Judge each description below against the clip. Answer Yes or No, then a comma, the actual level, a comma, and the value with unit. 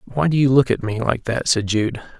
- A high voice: No, low, 125 Hz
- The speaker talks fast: Yes, fast, 275 wpm